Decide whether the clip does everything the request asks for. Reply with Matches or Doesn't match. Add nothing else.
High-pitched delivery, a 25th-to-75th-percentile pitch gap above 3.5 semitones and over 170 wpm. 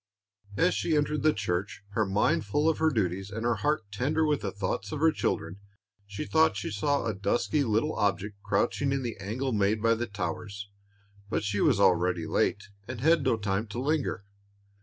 Doesn't match